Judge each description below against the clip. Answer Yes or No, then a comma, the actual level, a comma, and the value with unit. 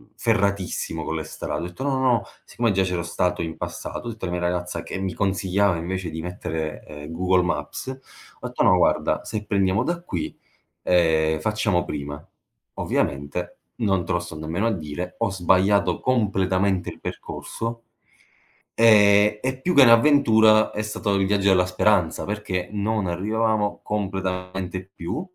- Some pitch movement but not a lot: Yes, average, 3.4 semitones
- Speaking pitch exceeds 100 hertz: No, very low, 95 Hz